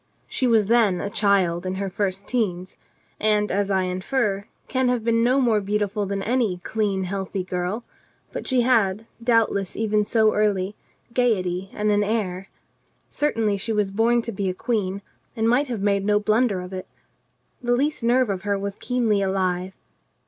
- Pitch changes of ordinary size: Yes, average, 3.0 semitones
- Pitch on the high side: Yes, high, 205 Hz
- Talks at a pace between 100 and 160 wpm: No, average, 175 wpm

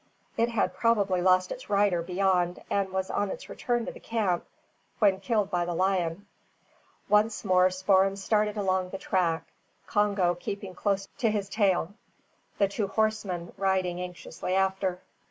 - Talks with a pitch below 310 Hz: Yes, high, 190 Hz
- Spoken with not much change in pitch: Yes, narrow, 2.2 semitones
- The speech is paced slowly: No, average, 155 wpm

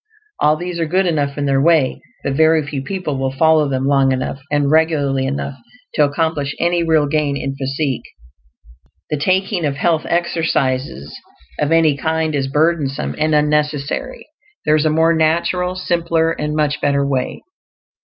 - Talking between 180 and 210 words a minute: No, average, 165 wpm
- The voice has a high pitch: No, medium, 150 Hz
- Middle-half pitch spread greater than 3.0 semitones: No, average, 2.7 semitones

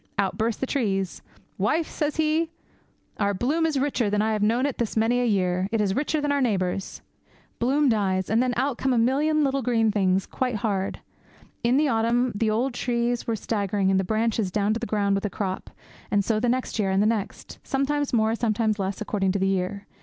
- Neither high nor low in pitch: No, high, 225 Hz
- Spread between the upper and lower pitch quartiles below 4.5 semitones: Yes, average, 4.1 semitones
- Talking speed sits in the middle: No, fast, 220 wpm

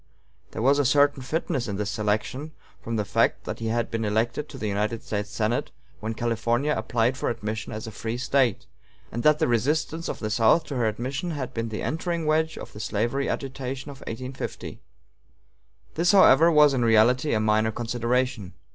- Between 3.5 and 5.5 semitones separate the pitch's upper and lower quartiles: Yes, average, 4.2 semitones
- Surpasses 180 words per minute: Yes, average, 190 wpm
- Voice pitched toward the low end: Yes, low, 120 Hz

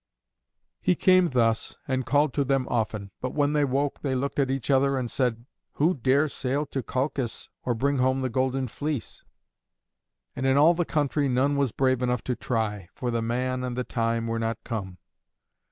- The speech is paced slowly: No, average, 190 wpm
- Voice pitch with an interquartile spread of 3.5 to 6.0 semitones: No, average, 2.9 semitones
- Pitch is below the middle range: Yes, low, 130 Hz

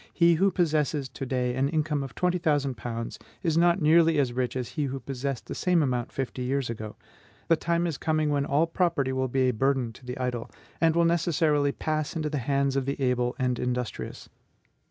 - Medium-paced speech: No, fast, 210 wpm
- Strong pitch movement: No, average, 4.0 semitones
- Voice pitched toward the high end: No, medium, 140 Hz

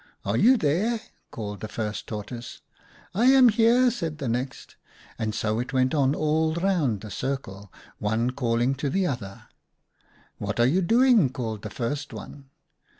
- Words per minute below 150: No, average, 185 wpm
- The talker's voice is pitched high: No, low, 135 Hz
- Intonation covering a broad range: Yes, wide, 7.4 semitones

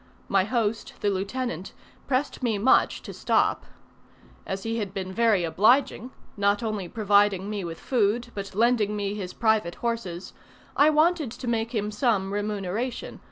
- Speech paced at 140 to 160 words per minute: Yes, average, 155 wpm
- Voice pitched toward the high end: Yes, high, 210 Hz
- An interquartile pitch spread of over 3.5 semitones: No, average, 3.2 semitones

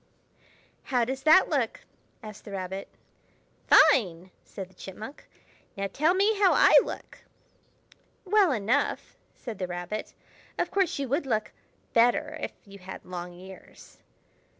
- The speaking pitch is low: No, high, 220 Hz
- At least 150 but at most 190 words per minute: No, slow, 135 wpm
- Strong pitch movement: Yes, wide, 7.1 semitones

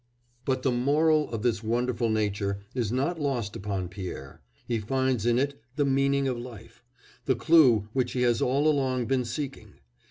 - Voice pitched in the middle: No, low, 125 Hz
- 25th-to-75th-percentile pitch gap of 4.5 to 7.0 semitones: No, average, 3.7 semitones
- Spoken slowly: No, average, 170 wpm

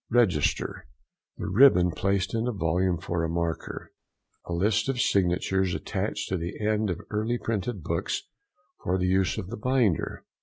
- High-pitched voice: No, very low, 95 Hz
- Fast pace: No, average, 155 wpm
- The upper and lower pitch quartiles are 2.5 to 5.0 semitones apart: Yes, average, 3.7 semitones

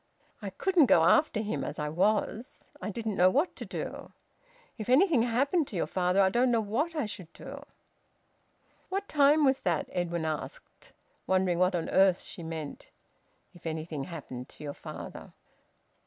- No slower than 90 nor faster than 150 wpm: No, average, 170 wpm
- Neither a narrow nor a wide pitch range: No, wide, 7.7 semitones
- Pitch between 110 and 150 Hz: No, high, 195 Hz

